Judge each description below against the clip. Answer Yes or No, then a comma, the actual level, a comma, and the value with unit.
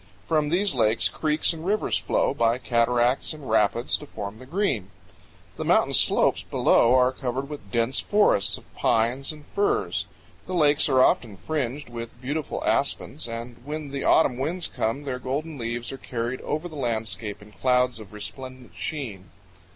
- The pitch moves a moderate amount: Yes, average, 4.4 semitones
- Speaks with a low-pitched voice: Yes, low, 130 Hz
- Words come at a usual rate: Yes, average, 165 wpm